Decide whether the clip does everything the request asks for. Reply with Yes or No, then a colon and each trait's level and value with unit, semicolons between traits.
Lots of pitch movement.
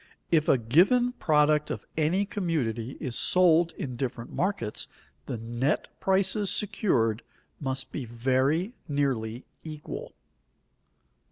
Yes: wide, 6.6 semitones